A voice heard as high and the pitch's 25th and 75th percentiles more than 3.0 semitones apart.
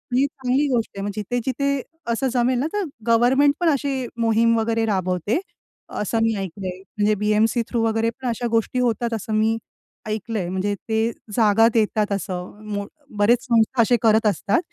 No: high, 225 Hz; average, 2.7 semitones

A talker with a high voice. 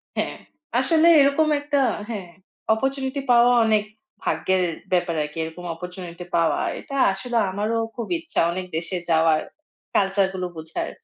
Yes: high, 195 Hz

